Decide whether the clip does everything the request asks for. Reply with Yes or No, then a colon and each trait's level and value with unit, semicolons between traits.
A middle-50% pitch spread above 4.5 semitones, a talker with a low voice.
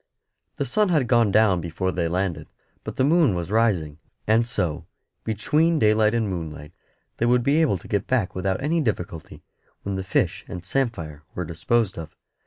Yes: wide, 5.5 semitones; low, 100 Hz